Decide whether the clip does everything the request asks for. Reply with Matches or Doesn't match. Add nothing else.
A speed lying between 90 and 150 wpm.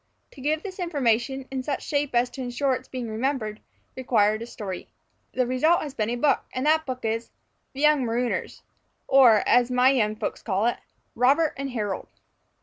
Doesn't match